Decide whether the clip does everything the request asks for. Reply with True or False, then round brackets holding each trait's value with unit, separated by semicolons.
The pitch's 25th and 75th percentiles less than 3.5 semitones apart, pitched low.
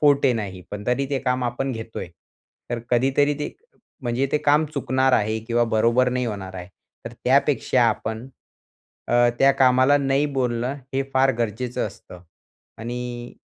True (2.7 semitones; 125 Hz)